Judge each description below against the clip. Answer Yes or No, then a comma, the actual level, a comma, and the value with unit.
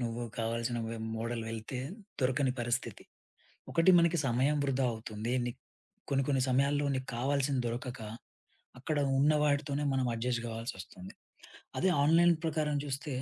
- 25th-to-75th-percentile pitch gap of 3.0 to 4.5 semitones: Yes, average, 3.6 semitones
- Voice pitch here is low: Yes, low, 130 Hz